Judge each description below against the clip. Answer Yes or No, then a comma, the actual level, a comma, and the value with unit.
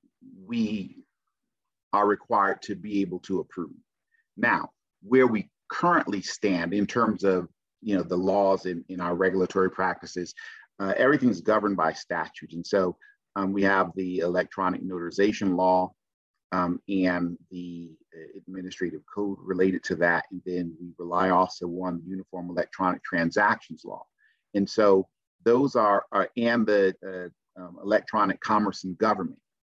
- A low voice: Yes, very low, 95 Hz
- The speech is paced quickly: No, average, 145 wpm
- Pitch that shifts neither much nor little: No, narrow, 1.9 semitones